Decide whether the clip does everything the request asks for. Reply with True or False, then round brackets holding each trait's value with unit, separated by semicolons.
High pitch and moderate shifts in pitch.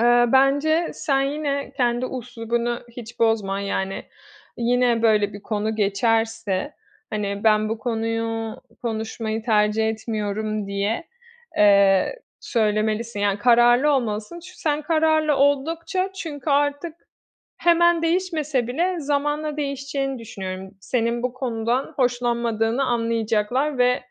True (240 Hz; 4.5 semitones)